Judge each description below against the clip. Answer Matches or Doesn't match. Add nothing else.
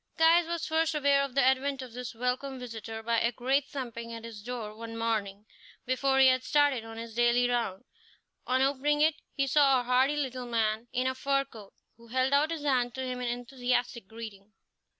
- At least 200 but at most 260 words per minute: Matches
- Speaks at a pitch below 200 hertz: Doesn't match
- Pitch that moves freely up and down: Doesn't match